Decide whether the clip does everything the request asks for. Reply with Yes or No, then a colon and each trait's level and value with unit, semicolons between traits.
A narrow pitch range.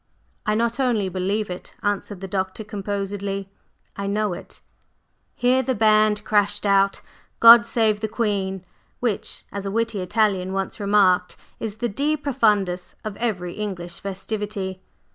Yes: narrow, 2.3 semitones